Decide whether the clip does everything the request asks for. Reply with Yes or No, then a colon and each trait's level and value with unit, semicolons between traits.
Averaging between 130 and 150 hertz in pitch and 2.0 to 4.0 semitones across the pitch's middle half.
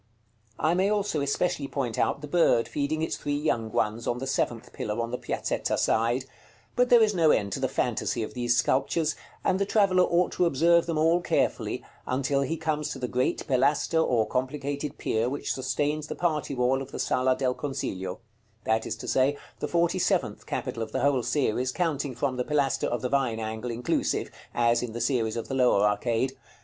No: low, 135 Hz; average, 4.5 semitones